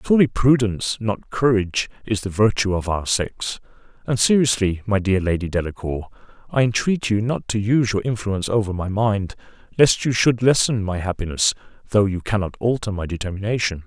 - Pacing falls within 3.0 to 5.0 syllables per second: No, 5.5 syllables/s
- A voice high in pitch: No, low, 105 Hz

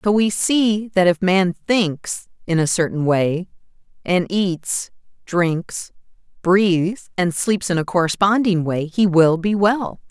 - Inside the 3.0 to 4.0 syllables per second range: Yes, 3.6 syllables/s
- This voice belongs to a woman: Yes, female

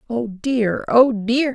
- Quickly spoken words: No, average, 155 wpm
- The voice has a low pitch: No, high, 235 Hz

